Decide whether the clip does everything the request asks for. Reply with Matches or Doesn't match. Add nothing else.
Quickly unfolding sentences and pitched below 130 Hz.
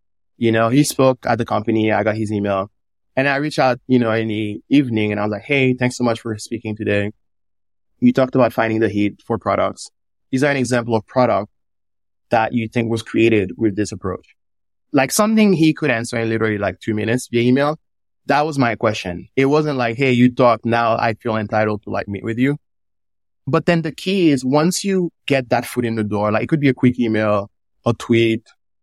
Matches